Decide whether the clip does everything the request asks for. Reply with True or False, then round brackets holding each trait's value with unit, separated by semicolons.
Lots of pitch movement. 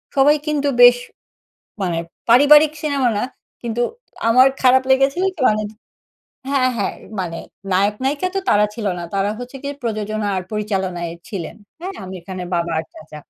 True (6.2 semitones)